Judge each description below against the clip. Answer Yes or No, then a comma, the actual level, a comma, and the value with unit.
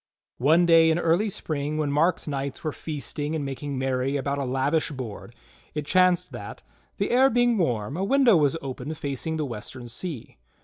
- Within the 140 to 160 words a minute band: No, average, 180 wpm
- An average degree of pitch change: Yes, average, 3.9 semitones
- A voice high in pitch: No, medium, 150 Hz